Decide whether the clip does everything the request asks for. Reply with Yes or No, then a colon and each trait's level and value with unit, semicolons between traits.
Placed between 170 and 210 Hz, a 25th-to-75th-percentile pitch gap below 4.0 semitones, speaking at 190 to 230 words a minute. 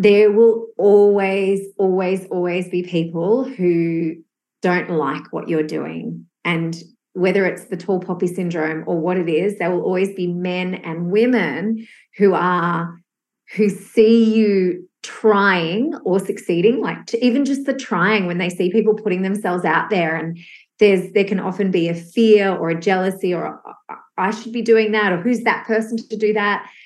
No: high, 190 Hz; average, 3.5 semitones; average, 175 wpm